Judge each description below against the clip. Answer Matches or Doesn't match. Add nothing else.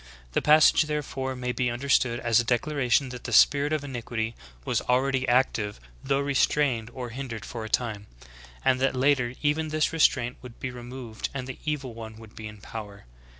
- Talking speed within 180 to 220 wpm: Matches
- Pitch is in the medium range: Doesn't match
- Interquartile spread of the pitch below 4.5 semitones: Matches